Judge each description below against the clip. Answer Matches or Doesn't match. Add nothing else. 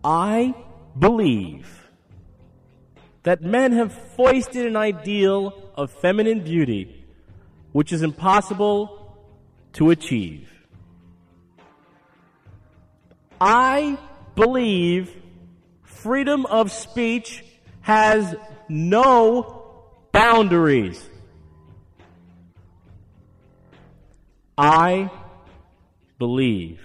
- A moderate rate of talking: Doesn't match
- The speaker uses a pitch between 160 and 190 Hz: Doesn't match